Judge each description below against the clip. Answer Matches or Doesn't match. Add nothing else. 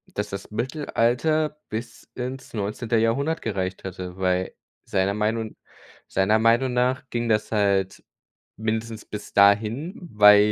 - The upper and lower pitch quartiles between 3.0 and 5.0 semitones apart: Matches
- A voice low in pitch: Matches